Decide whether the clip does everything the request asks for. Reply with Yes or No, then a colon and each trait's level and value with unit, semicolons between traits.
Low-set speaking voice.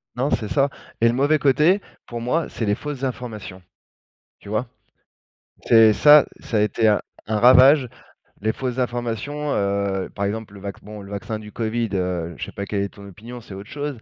Yes: low, 115 Hz